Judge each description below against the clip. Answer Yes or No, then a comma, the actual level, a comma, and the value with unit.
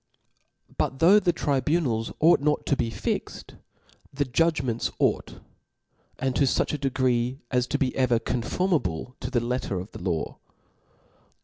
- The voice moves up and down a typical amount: Yes, average, 3.9 semitones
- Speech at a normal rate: Yes, average, 145 wpm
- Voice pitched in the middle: No, low, 130 Hz